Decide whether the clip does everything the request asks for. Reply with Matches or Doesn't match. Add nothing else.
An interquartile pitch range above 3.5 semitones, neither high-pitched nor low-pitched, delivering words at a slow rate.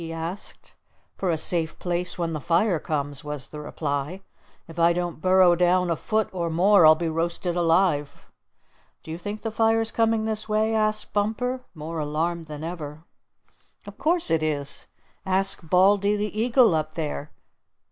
Doesn't match